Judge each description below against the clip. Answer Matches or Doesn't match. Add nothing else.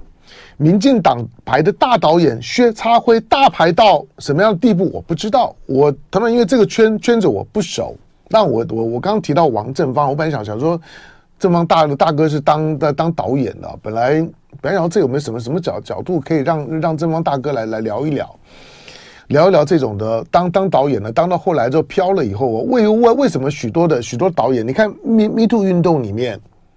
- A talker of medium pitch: Matches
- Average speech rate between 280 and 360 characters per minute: Matches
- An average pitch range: Doesn't match